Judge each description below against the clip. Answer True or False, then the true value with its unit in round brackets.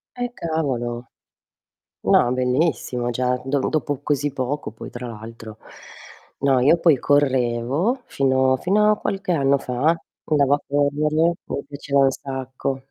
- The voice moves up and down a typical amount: True (3.1 semitones)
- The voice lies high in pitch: False (135 Hz)